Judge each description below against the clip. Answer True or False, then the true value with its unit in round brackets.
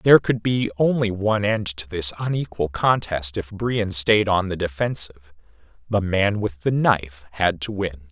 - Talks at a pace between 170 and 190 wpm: True (180 wpm)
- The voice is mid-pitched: False (95 Hz)